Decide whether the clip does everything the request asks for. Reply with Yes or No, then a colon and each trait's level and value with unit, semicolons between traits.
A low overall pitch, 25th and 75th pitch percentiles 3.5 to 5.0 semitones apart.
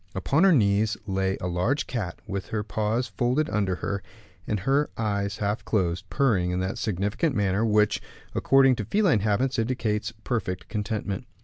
Yes: low, 105 Hz; average, 3.8 semitones